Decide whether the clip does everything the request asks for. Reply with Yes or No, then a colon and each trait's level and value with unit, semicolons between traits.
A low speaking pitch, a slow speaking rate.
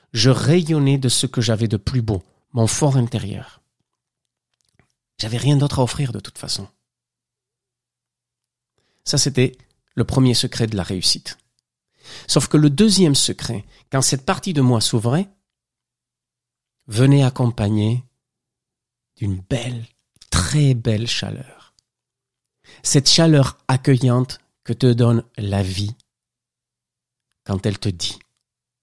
Yes: low, 125 Hz; slow, 120 wpm